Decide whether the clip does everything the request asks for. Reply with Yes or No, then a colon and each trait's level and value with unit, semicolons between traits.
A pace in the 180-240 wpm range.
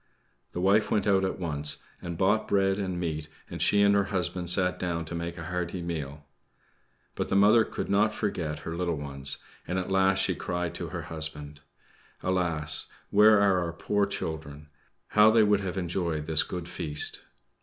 Yes: average, 185 wpm